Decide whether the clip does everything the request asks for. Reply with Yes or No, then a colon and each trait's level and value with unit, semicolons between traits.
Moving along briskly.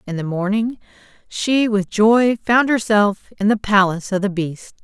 No: average, 175 wpm